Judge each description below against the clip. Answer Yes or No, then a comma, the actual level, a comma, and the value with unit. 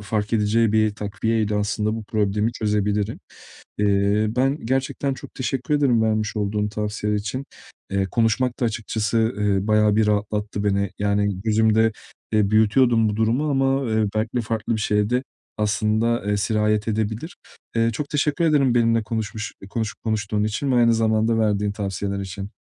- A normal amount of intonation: No, narrow, 1.8 semitones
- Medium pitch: No, low, 110 Hz